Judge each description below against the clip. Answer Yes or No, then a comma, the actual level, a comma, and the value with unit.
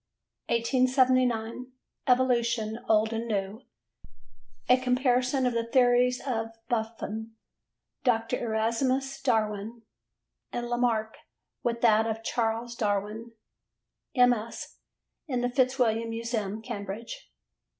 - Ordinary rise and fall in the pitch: No, narrow, 2.1 semitones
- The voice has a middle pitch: No, high, 235 Hz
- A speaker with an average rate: No, slow, 95 wpm